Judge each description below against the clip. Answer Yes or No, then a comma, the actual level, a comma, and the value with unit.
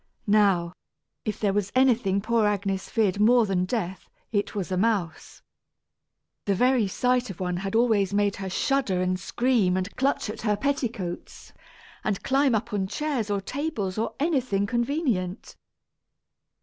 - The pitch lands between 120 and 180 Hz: No, high, 210 Hz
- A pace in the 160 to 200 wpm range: No, average, 150 wpm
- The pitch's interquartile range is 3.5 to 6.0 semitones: Yes, average, 4.2 semitones